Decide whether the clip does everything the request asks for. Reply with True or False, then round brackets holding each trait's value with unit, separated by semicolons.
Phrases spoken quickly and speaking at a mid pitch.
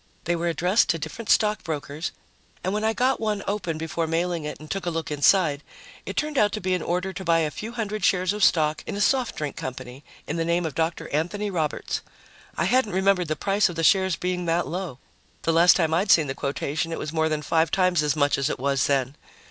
True (240 wpm; 170 Hz)